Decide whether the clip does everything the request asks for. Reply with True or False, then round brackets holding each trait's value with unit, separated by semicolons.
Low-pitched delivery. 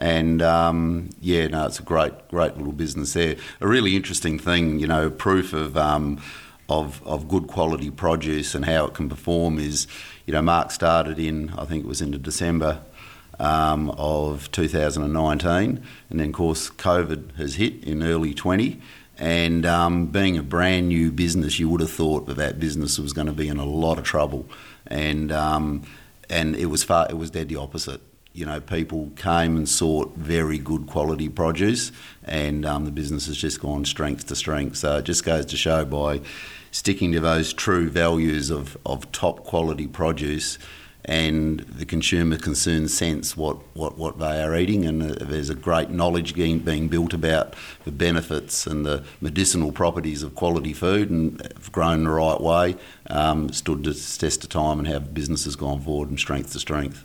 True (80 Hz)